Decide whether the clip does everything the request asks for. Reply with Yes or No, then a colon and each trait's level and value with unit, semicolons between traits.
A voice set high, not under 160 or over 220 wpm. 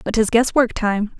Yes: high, 220 Hz; average, 200 wpm